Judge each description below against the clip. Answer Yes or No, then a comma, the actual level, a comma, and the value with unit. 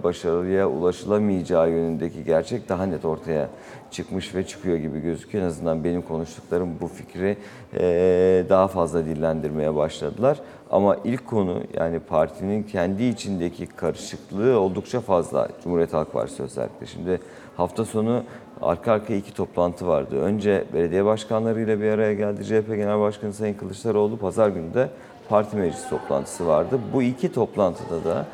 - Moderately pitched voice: No, very low, 95 Hz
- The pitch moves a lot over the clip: No, average, 4.1 semitones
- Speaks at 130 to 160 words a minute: Yes, fast, 140 wpm